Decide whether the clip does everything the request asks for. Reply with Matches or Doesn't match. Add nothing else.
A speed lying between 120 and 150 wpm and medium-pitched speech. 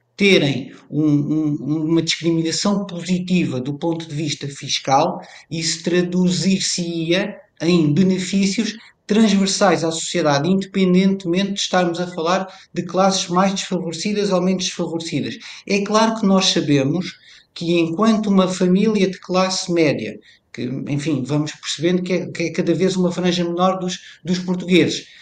Matches